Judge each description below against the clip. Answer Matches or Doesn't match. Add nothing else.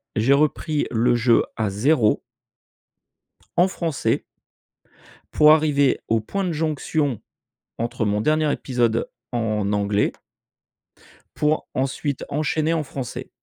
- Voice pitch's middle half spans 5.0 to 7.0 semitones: Matches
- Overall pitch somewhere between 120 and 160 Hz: Matches